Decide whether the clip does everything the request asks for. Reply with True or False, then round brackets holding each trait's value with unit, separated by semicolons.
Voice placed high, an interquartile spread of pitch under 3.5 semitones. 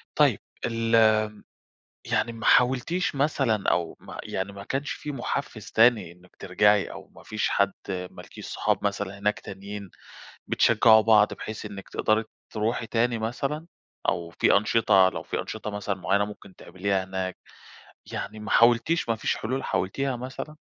False (110 Hz; 3.1 semitones)